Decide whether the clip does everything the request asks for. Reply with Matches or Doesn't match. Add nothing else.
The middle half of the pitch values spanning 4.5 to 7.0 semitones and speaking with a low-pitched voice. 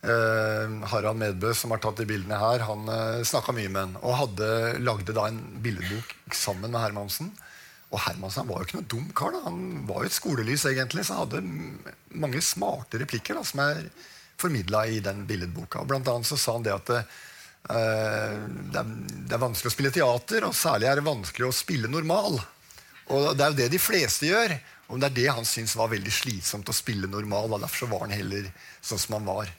Doesn't match